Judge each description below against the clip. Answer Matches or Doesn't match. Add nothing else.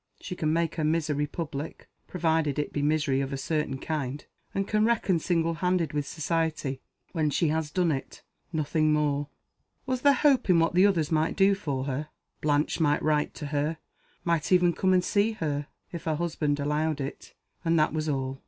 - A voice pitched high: Doesn't match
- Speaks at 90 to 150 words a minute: Doesn't match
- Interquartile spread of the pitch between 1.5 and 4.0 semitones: Matches